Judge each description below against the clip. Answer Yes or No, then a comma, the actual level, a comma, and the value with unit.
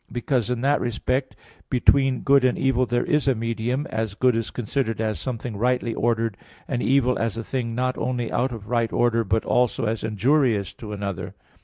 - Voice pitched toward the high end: No, low, 120 Hz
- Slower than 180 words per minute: No, average, 190 wpm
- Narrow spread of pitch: Yes, narrow, 2.2 semitones